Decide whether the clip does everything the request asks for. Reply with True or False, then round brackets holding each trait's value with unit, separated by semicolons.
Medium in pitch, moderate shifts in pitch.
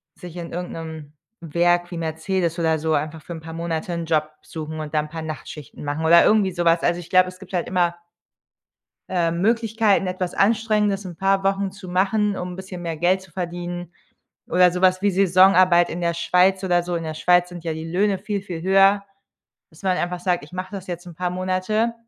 False (180 Hz; 2.3 semitones)